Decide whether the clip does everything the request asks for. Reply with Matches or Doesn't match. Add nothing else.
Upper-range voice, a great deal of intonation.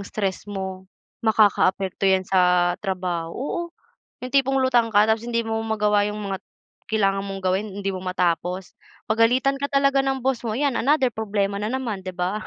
Doesn't match